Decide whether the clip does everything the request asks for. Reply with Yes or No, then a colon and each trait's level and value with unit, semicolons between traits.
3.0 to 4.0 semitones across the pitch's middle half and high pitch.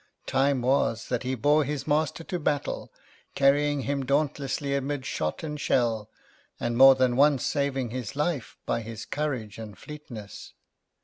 No: average, 3.3 semitones; low, 135 Hz